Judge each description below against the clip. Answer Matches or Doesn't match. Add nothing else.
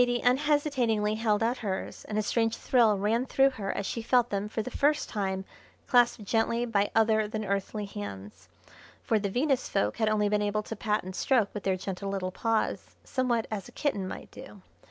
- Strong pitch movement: Doesn't match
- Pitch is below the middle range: Doesn't match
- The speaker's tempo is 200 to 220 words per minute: Matches